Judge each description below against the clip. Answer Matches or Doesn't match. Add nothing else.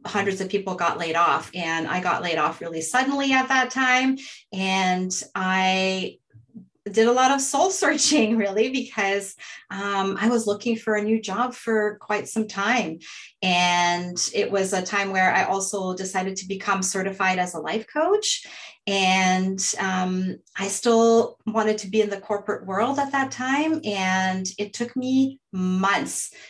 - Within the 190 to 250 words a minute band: Doesn't match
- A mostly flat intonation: Doesn't match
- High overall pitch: Matches